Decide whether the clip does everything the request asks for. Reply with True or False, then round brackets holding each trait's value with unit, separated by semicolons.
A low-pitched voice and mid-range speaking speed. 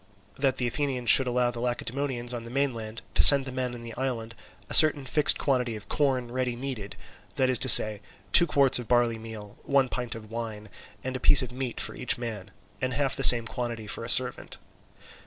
False (125 Hz; 215 wpm)